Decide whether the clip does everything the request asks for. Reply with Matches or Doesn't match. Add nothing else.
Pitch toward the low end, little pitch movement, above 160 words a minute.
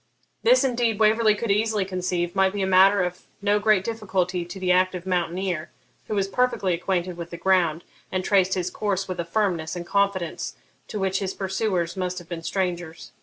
Doesn't match